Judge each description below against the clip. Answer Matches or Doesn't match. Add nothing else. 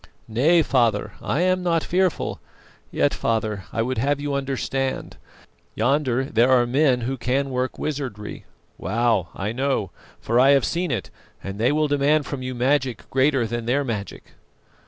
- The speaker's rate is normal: Matches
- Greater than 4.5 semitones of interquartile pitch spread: Doesn't match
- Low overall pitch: Matches